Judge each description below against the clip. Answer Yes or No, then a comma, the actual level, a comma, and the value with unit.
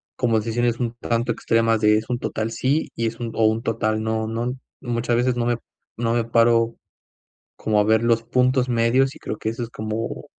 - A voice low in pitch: Yes, low, 115 Hz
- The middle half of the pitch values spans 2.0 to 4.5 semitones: No, narrow, 1.4 semitones